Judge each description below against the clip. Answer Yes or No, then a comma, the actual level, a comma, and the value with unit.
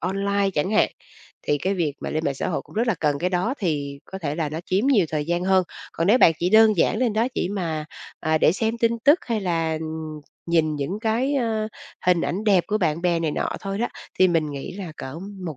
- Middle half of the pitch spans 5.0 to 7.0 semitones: Yes, average, 5.3 semitones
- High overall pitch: No, medium, 180 Hz